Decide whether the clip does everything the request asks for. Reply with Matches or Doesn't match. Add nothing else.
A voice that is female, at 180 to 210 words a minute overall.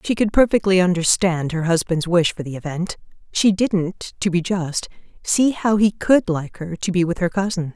Matches